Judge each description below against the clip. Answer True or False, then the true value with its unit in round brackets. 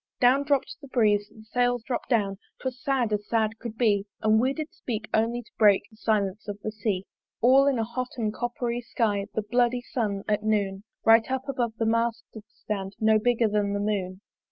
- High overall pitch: True (225 Hz)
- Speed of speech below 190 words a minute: False (205 wpm)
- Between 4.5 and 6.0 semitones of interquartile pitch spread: False (2.8 semitones)